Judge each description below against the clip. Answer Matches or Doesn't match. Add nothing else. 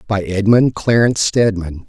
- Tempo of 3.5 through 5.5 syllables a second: Matches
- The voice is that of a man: Matches